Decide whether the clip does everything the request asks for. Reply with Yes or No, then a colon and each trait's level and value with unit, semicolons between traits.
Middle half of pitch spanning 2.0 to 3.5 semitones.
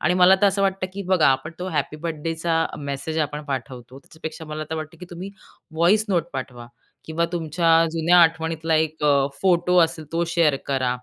Yes: average, 2.7 semitones